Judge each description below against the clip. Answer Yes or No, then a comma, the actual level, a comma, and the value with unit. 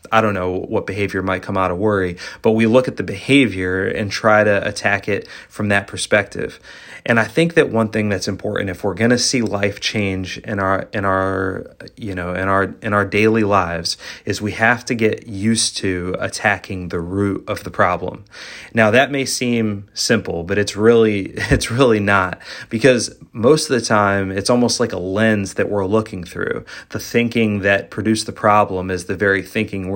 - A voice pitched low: Yes, low, 105 Hz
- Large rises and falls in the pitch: No, average, 2.7 semitones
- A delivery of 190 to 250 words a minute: Yes, average, 200 wpm